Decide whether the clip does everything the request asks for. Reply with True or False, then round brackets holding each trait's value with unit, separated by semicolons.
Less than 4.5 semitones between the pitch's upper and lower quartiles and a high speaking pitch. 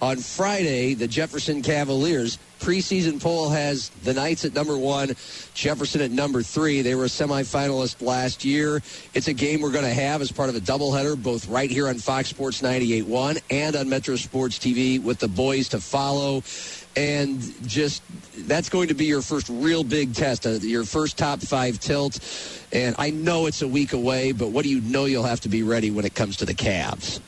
False (2.8 semitones; 135 Hz)